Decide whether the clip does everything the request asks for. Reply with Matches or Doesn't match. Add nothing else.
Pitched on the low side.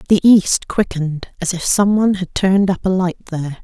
Doesn't match